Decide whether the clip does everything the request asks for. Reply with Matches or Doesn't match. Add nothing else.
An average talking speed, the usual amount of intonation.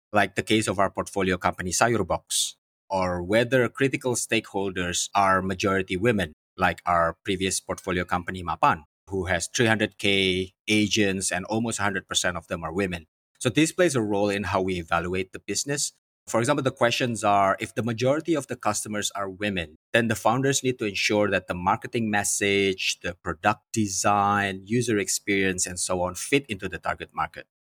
Matches